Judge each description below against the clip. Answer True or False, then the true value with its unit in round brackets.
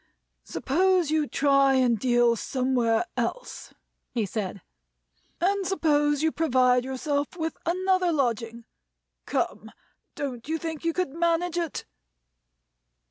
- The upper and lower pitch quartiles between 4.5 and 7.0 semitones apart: True (5.1 semitones)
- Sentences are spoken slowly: True (115 wpm)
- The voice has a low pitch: False (290 Hz)